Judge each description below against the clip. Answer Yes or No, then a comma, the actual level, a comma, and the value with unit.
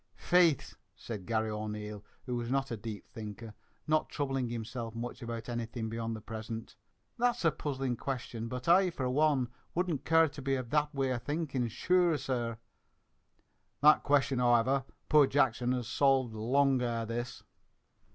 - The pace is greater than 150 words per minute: Yes, average, 160 wpm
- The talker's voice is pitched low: Yes, low, 125 Hz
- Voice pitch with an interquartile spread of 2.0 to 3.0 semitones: No, average, 3.7 semitones